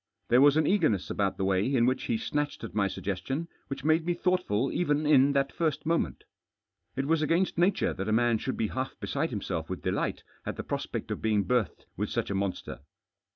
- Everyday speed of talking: No, fast, 215 wpm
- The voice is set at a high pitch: No, low, 135 Hz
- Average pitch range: No, wide, 6.5 semitones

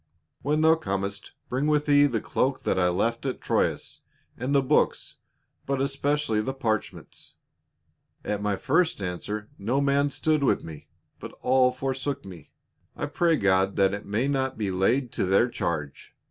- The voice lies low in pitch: Yes, low, 125 Hz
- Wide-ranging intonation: Yes, wide, 5.9 semitones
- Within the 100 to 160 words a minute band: No, average, 170 wpm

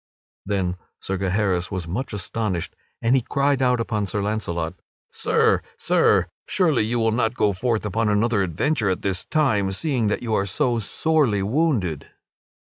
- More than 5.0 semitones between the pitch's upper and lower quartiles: No, average, 4.4 semitones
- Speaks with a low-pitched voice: Yes, low, 105 Hz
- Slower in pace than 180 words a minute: Yes, average, 165 wpm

